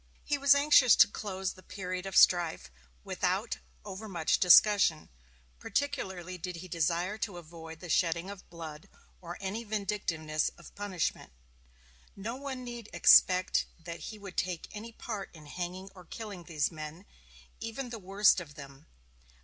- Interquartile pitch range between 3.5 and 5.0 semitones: Yes, average, 3.8 semitones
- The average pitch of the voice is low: No, medium, 185 Hz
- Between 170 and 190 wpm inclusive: No, average, 150 wpm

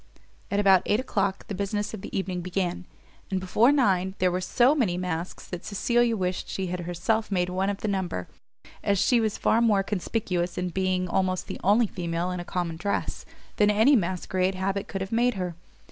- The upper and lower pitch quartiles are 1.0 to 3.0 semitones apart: Yes, narrow, 2.5 semitones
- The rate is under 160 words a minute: No, average, 200 wpm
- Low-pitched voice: No, high, 190 Hz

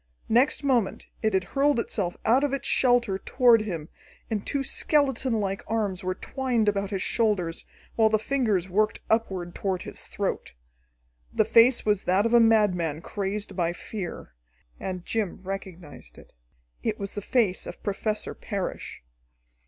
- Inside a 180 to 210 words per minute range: No, average, 150 wpm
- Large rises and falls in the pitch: No, average, 3.6 semitones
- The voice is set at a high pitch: Yes, high, 210 Hz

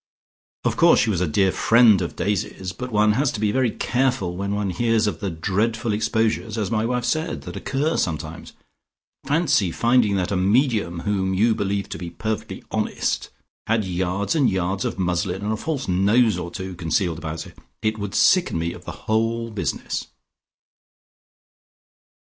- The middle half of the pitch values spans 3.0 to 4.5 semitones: Yes, average, 3.9 semitones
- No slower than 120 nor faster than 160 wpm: No, average, 175 wpm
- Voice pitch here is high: No, low, 105 Hz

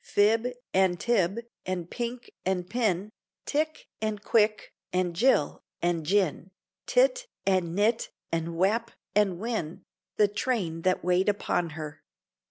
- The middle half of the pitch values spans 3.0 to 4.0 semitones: No, average, 4.5 semitones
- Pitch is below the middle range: No, high, 195 Hz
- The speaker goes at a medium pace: No, slow, 130 wpm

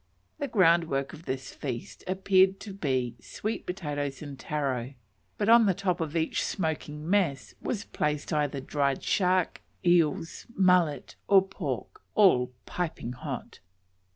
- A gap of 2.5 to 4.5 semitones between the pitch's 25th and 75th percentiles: No, average, 5.2 semitones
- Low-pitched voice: No, medium, 165 Hz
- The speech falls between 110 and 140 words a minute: Yes, slow, 135 wpm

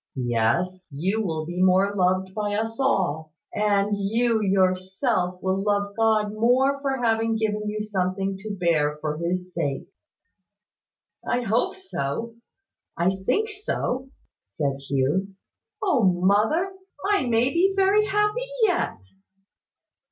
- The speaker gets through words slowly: Yes, slow, 125 wpm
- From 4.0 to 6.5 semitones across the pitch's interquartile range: Yes, average, 4.6 semitones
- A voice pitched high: Yes, high, 205 Hz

